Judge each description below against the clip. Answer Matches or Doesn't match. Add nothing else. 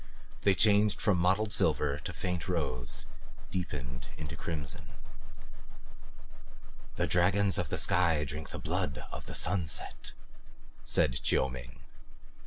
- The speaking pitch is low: Matches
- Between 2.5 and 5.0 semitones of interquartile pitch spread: Doesn't match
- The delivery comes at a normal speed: Doesn't match